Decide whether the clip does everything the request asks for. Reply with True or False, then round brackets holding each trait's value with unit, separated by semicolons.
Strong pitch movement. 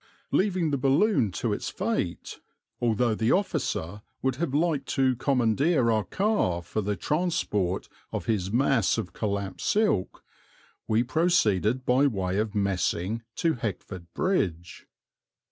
True (6.4 semitones)